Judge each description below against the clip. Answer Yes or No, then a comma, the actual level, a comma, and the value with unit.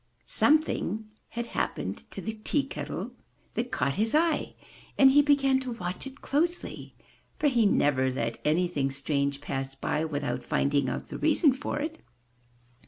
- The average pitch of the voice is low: No, high, 220 Hz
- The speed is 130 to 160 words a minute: Yes, average, 155 wpm